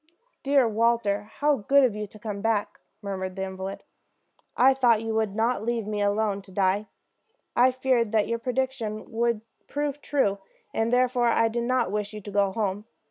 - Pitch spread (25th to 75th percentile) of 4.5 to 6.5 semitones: No, average, 3.2 semitones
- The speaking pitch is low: No, high, 225 Hz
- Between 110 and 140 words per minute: No, average, 185 wpm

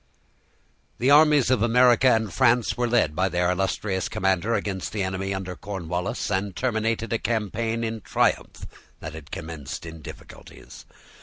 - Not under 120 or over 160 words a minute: Yes, average, 150 wpm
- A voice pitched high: No, low, 105 Hz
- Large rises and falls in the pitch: No, average, 4.2 semitones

